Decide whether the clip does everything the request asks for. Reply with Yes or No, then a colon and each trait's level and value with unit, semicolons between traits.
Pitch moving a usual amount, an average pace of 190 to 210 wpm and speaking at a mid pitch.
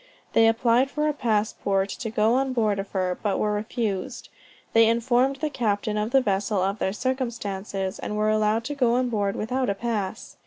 No: average, 3.3 semitones; average, 195 wpm; high, 220 Hz